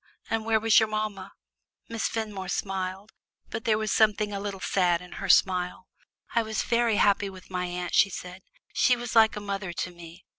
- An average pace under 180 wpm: No, average, 195 wpm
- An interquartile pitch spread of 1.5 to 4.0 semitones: Yes, average, 3.0 semitones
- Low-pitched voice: No, high, 200 Hz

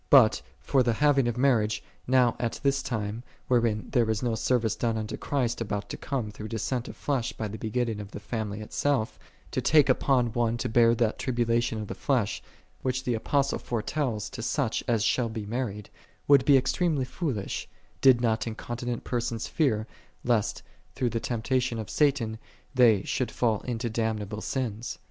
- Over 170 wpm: Yes, average, 180 wpm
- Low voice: Yes, low, 120 Hz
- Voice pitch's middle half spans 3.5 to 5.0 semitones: No, average, 2.8 semitones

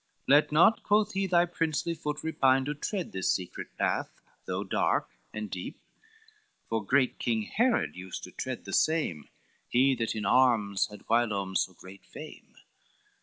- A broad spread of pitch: Yes, wide, 7.6 semitones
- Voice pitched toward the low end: Yes, low, 130 Hz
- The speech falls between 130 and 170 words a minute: Yes, average, 160 wpm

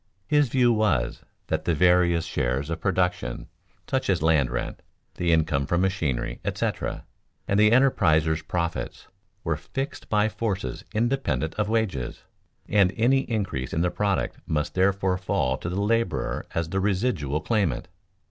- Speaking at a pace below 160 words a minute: Yes, average, 150 wpm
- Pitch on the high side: No, very low, 95 Hz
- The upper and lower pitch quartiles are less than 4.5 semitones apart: No, average, 5.2 semitones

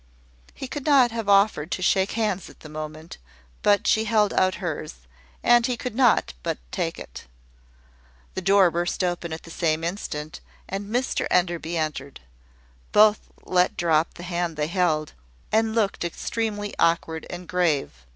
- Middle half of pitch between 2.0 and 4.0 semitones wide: No, average, 4.5 semitones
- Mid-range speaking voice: Yes, medium, 180 Hz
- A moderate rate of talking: Yes, average, 160 wpm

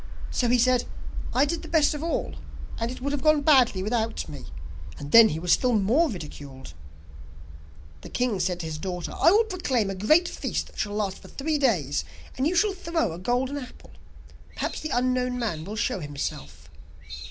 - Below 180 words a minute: No, average, 195 wpm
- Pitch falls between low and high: No, high, 240 Hz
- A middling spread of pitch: No, wide, 8.1 semitones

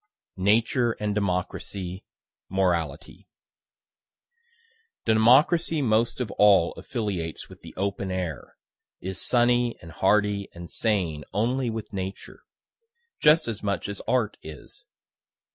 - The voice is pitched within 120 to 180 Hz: No, low, 100 Hz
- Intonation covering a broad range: No, average, 4.0 semitones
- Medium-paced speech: No, slow, 110 wpm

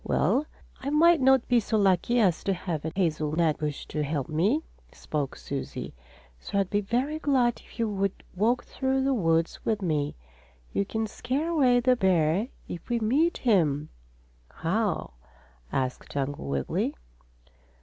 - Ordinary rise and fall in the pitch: No, wide, 7.8 semitones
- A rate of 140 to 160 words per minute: Yes, average, 155 wpm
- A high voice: Yes, high, 200 Hz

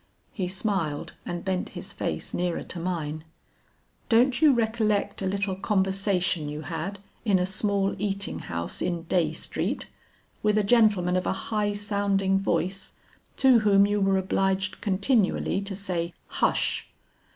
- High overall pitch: Yes, high, 195 Hz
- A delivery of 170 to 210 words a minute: No, average, 145 wpm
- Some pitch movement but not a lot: No, narrow, 2.3 semitones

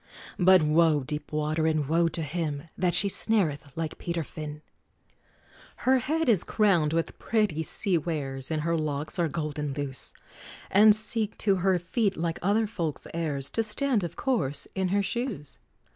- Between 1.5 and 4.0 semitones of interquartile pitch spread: No, average, 4.9 semitones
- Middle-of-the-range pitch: Yes, medium, 165 Hz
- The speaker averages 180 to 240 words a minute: No, average, 165 wpm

